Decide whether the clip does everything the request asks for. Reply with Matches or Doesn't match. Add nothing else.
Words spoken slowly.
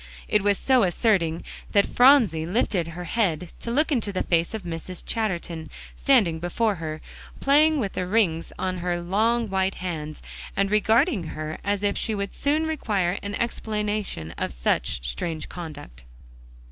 Doesn't match